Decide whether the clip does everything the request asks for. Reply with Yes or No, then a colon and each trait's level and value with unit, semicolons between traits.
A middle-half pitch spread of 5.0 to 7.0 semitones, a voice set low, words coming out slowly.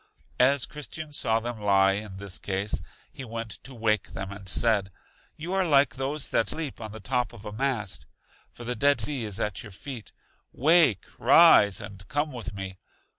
No: average, 5.3 semitones; low, 115 Hz; average, 185 wpm